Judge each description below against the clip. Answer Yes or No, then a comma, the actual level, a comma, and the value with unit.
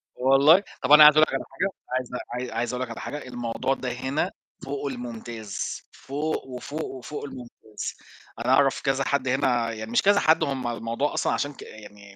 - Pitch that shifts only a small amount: No, average, 3.1 semitones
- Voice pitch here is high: No, low, 130 Hz